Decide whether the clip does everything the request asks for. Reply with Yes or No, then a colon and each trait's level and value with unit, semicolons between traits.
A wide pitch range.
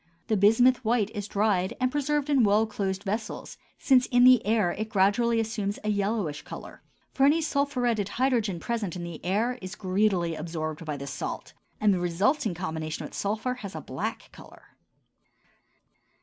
No: average, 4.6 semitones